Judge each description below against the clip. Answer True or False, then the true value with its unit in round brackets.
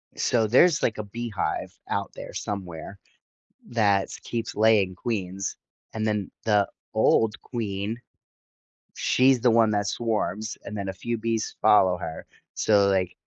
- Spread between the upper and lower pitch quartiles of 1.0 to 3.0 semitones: True (2.6 semitones)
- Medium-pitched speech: False (105 Hz)